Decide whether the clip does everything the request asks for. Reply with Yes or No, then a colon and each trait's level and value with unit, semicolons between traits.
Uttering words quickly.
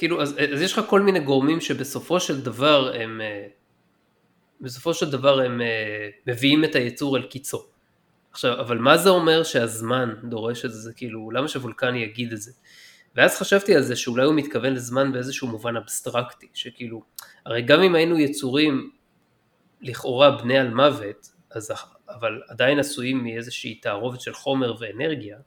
Yes: fast, 155 wpm